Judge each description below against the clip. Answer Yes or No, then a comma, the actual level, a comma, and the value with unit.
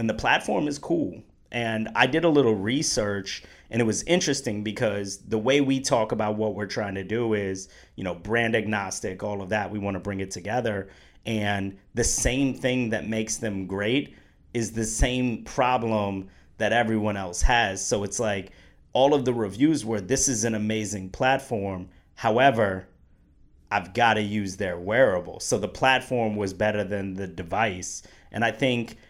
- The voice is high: No, low, 105 Hz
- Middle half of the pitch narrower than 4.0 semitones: Yes, average, 3.3 semitones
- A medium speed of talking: Yes, average, 180 wpm